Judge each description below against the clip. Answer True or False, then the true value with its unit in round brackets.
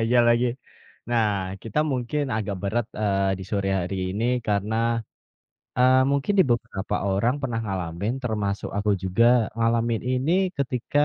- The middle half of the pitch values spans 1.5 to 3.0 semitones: False (3.4 semitones)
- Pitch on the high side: False (115 Hz)